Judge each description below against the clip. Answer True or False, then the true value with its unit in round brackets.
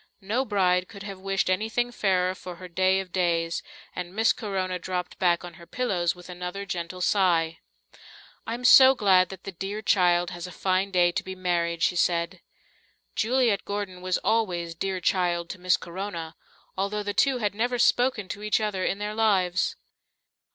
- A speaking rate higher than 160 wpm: True (180 wpm)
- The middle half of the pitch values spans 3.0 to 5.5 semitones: False (2.5 semitones)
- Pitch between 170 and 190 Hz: True (185 Hz)